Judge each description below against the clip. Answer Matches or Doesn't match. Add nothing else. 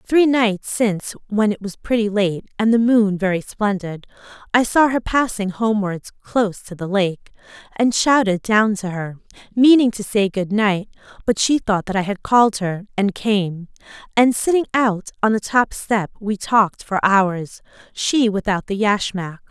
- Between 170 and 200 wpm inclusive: Matches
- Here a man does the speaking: Doesn't match